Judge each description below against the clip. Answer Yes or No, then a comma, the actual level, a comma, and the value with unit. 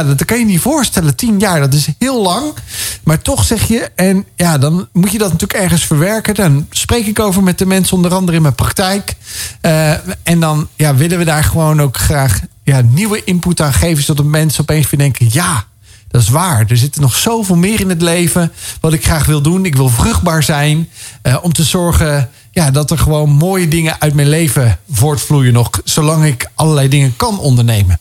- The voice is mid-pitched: Yes, medium, 155 Hz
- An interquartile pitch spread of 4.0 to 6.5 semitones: Yes, average, 4.9 semitones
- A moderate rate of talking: No, fast, 215 wpm